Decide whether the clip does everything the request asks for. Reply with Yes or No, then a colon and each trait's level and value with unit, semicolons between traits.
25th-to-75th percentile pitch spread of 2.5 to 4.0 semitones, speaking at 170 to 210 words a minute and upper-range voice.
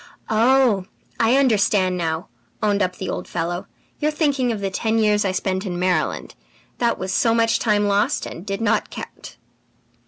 Yes: average, 3.6 semitones; average, 180 wpm; high, 205 Hz